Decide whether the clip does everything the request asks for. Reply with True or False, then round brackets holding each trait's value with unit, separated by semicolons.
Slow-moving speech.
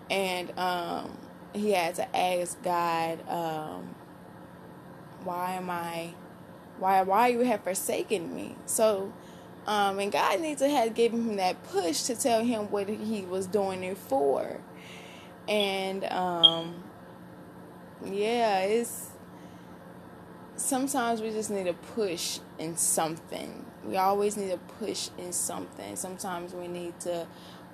True (130 wpm)